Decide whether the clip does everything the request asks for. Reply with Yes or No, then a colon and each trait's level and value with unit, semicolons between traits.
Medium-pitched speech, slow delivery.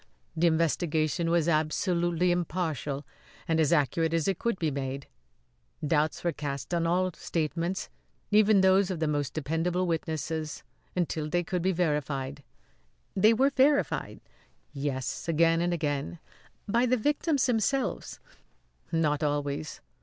Yes: medium, 165 Hz; slow, 130 wpm